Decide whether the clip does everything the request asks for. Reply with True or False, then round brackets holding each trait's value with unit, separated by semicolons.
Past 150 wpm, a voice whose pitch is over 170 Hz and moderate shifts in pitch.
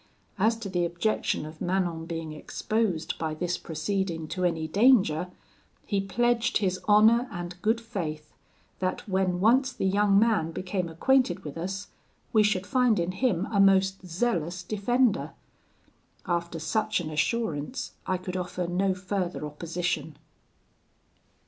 False (140 wpm; 185 Hz; 3.9 semitones)